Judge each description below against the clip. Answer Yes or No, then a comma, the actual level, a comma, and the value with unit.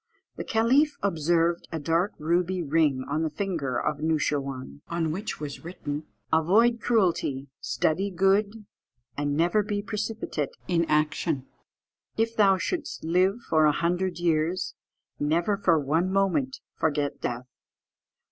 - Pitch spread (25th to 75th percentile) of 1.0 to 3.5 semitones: No, average, 4.6 semitones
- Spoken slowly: Yes, slow, 130 wpm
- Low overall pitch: No, medium, 170 Hz